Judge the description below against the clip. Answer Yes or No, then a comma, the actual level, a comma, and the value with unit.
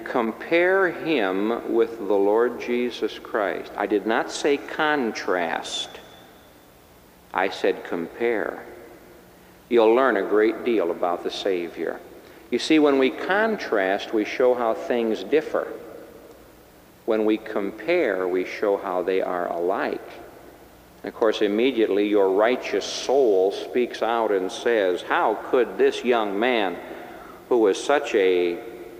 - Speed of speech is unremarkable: No, slow, 130 wpm